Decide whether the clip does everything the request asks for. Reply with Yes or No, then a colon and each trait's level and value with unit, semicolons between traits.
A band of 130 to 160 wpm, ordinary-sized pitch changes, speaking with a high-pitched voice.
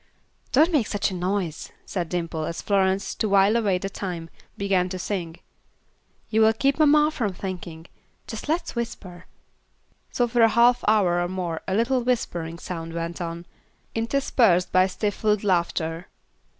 Yes: average, 155 wpm; average, 4.5 semitones; high, 195 Hz